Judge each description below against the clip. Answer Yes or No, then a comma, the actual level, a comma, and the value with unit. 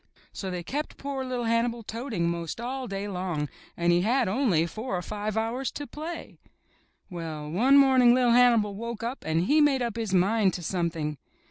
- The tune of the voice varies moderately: No, wide, 6.0 semitones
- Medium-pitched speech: No, high, 220 Hz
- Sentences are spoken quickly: No, average, 190 wpm